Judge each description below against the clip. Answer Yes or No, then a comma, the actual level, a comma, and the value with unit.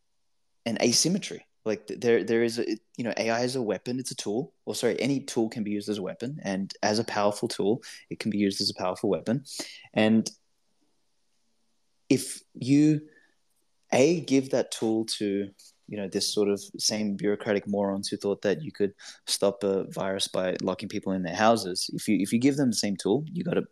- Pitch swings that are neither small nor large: Yes, average, 3.1 semitones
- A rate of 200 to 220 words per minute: Yes, fast, 205 wpm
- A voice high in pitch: No, low, 105 Hz